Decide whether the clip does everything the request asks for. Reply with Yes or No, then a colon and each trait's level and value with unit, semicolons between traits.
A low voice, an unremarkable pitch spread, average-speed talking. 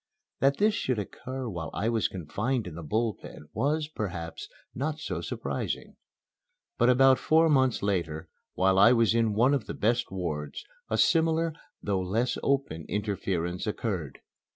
No: low, 110 Hz; wide, 6.5 semitones; average, 155 wpm